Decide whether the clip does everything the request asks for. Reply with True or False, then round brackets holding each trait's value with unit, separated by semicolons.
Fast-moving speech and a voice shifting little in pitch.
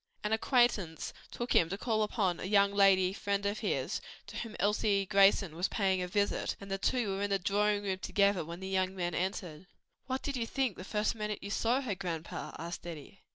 True (215 wpm; 2.3 semitones)